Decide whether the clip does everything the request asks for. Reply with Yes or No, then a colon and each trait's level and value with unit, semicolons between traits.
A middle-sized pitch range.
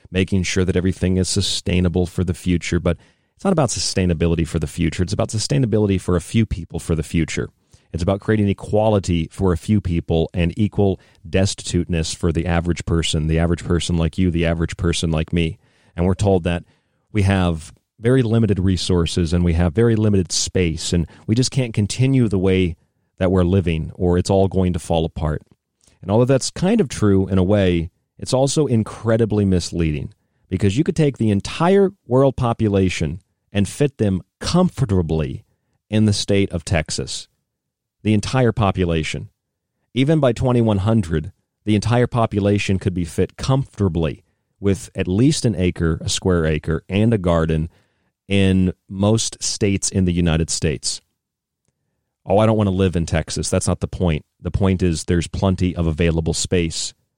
Yes: average, 4.0 semitones